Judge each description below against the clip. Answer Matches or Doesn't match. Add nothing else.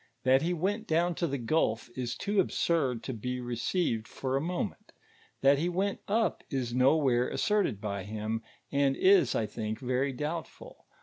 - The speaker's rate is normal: Matches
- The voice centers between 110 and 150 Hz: Matches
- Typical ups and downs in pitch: Doesn't match